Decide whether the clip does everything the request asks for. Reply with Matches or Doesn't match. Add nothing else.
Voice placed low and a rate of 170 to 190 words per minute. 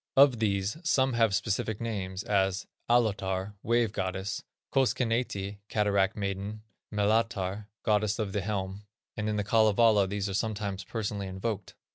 Doesn't match